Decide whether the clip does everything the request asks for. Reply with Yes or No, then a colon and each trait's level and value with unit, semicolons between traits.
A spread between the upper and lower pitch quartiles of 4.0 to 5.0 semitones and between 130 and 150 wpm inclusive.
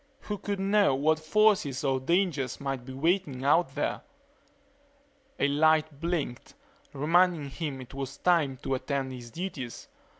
Yes: average, 4.5 semitones; average, 145 wpm